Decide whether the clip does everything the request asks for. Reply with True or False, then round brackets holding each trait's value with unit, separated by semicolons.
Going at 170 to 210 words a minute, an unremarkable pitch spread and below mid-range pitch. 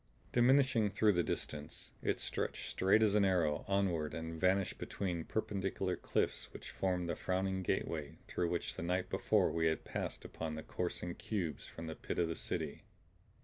True (175 wpm; 3.2 semitones; 90 Hz)